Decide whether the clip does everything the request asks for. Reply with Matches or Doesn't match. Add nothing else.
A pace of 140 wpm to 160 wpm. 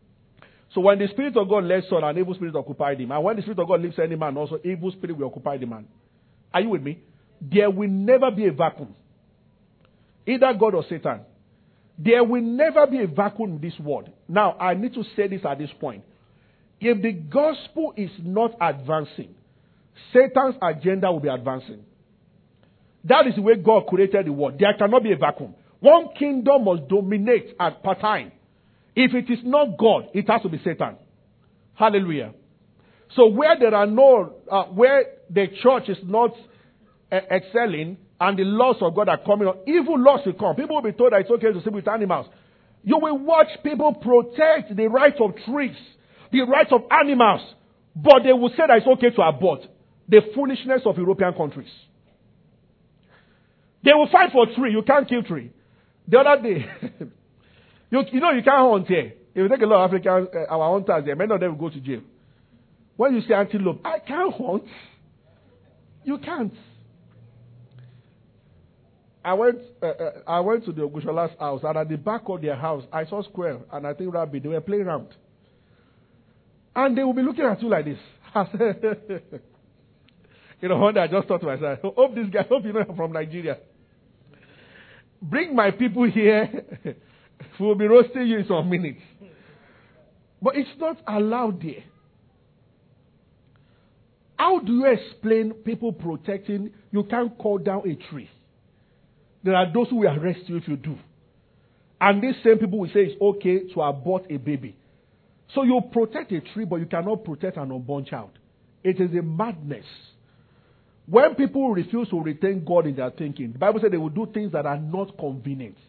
Doesn't match